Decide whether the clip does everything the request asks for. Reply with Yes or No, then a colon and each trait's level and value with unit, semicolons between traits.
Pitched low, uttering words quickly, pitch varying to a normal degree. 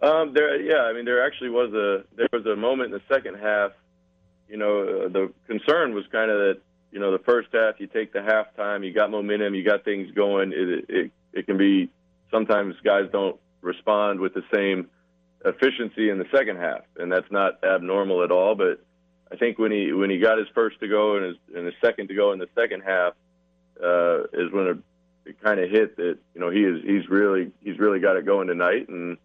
Yes: low, 100 Hz; fast, 225 wpm; average, 3.1 semitones